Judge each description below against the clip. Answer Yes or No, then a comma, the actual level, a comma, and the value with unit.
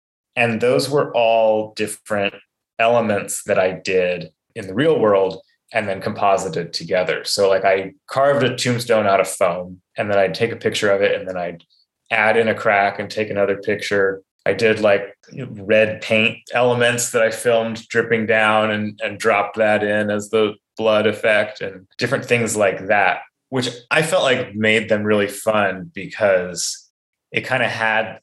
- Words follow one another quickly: No, average, 175 wpm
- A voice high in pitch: No, low, 110 Hz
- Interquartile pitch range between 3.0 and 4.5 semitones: No, narrow, 2.6 semitones